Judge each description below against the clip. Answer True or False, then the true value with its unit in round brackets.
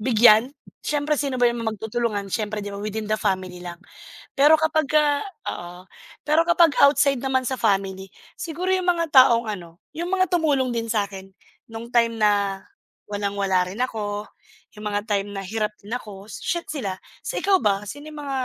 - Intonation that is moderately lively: False (6.0 semitones)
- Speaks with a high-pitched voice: True (225 Hz)